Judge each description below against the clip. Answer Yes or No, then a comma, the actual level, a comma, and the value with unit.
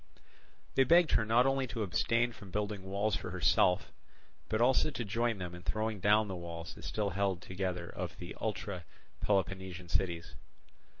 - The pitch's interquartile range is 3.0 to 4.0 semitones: Yes, average, 3.6 semitones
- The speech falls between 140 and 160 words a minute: No, average, 170 wpm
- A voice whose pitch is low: Yes, low, 100 Hz